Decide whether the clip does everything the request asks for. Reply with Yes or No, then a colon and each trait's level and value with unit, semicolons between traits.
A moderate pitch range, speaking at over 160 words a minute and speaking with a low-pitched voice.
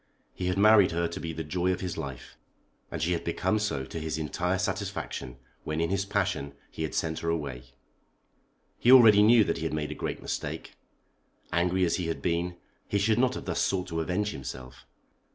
Yes: average, 3.8 semitones; fast, 205 wpm; very low, 85 Hz